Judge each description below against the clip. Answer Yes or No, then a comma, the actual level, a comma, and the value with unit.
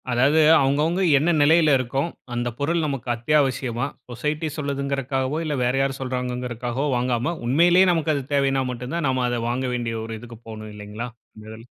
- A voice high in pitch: No, low, 130 Hz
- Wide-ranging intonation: No, average, 3.4 semitones